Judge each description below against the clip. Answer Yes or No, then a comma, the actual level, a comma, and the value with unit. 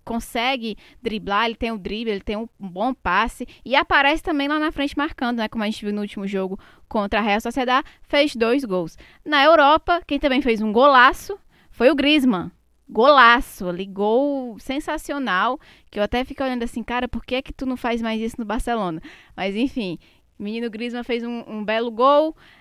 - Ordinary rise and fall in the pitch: Yes, average, 4.5 semitones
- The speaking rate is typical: No, fast, 195 wpm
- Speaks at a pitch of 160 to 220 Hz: No, high, 240 Hz